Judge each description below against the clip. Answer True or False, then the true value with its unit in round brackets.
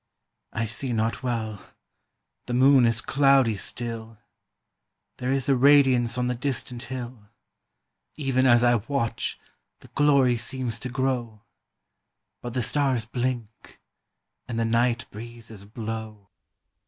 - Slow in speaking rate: True (125 wpm)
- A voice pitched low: True (120 Hz)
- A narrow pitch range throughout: True (2.3 semitones)